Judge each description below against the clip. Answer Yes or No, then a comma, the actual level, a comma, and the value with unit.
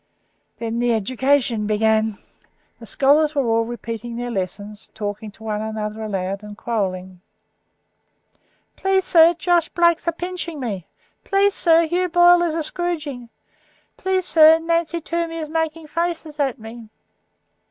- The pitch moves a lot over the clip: Yes, wide, 7.4 semitones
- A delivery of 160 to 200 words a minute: No, slow, 135 wpm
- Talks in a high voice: Yes, very high, 275 Hz